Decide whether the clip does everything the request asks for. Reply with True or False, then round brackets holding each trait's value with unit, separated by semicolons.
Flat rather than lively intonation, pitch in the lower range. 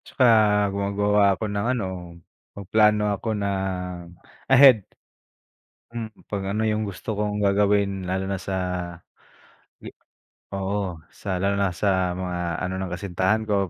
True (1.7 semitones; 100 Hz)